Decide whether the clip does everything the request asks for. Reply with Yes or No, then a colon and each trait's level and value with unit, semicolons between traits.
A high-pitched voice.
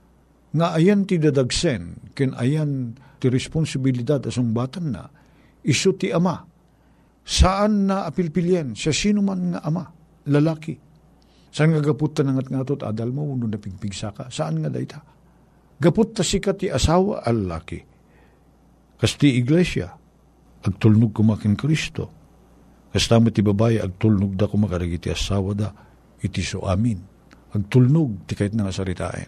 No: low, 135 Hz